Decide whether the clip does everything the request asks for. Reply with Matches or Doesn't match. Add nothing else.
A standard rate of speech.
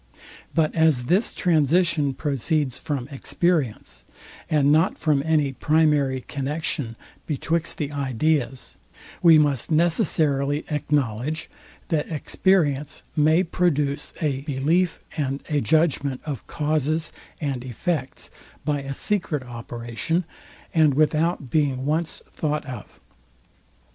Doesn't match